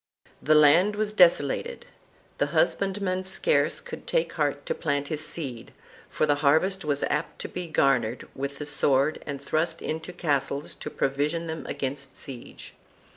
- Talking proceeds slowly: No, average, 160 wpm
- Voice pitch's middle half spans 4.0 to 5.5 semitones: Yes, average, 4.3 semitones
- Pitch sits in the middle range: Yes, medium, 150 Hz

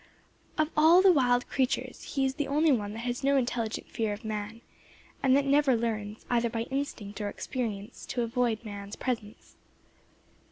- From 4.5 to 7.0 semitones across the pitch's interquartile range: No, average, 3.9 semitones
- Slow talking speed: No, average, 170 wpm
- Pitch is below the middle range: No, high, 240 Hz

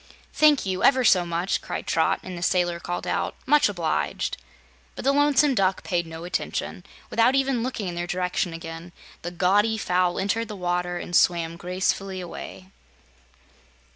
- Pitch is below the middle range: No, medium, 185 Hz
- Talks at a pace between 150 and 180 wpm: Yes, average, 165 wpm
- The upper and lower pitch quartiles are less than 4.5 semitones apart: Yes, average, 4.1 semitones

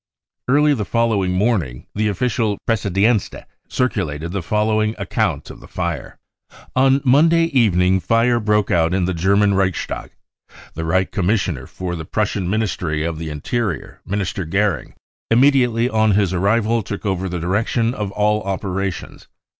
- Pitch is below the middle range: Yes, low, 100 Hz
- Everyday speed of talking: Yes, average, 150 wpm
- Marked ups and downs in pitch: No, average, 3.9 semitones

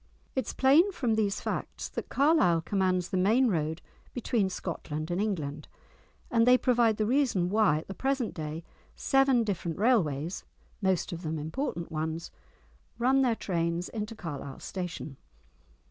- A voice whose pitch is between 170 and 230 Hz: Yes, high, 190 Hz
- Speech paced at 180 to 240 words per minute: No, average, 150 wpm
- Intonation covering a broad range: Yes, wide, 6.5 semitones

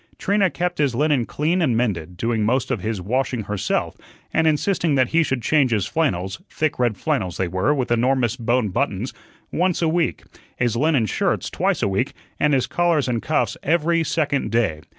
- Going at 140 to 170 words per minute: No, average, 190 wpm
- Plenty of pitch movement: Yes, wide, 6.0 semitones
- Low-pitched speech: Yes, low, 130 Hz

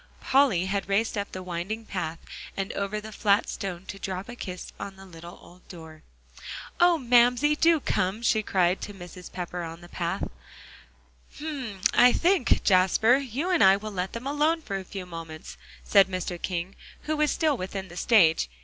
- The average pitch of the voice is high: Yes, high, 195 Hz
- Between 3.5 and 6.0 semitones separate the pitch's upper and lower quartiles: Yes, average, 5.1 semitones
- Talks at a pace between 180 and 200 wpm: Yes, average, 185 wpm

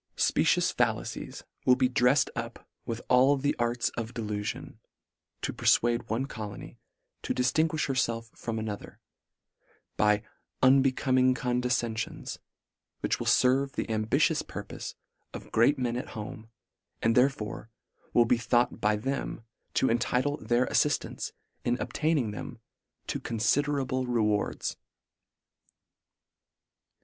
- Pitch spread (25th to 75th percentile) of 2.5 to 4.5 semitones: Yes, average, 2.8 semitones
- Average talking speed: No, slow, 120 wpm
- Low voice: Yes, low, 125 Hz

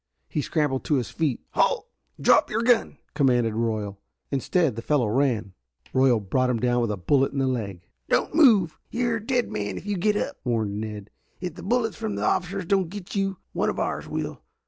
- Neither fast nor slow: No, fast, 210 wpm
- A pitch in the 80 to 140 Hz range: Yes, low, 135 Hz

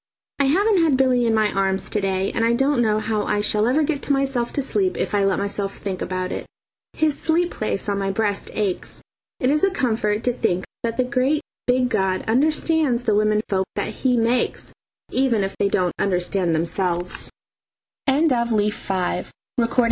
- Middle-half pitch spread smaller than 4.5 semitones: No, average, 5.2 semitones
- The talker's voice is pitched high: Yes, high, 225 Hz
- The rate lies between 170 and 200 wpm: Yes, average, 185 wpm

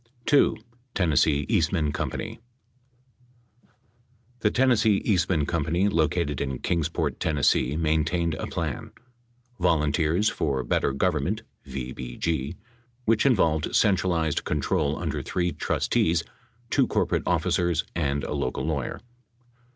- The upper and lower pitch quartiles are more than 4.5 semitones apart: No, average, 3.6 semitones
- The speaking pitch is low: Yes, very low, 80 Hz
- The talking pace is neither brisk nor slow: No, slow, 110 wpm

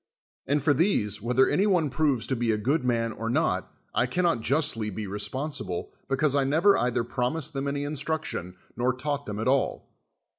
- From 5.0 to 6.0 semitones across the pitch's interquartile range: No, average, 4.5 semitones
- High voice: No, low, 130 Hz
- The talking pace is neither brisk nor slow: Yes, average, 185 wpm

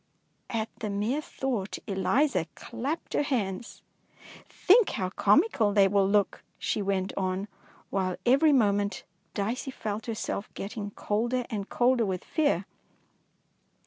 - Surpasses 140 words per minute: No, slow, 135 wpm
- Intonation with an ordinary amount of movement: Yes, average, 4.3 semitones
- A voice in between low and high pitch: No, high, 210 Hz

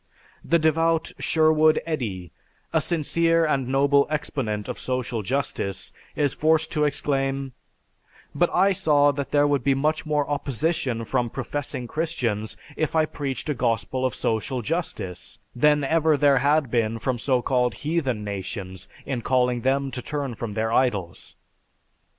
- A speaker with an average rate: Yes, average, 150 wpm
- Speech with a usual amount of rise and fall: Yes, average, 4.2 semitones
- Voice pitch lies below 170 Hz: Yes, low, 135 Hz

